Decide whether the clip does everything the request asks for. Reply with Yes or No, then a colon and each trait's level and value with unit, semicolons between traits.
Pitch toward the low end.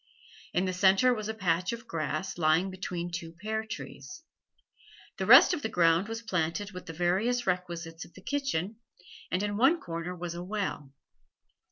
No: medium, 185 Hz